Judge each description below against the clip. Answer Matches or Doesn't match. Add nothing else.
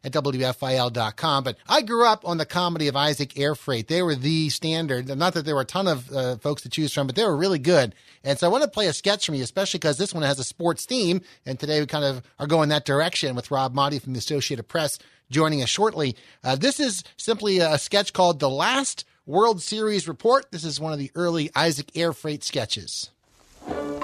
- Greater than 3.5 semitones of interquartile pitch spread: Matches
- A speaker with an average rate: Doesn't match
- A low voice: Doesn't match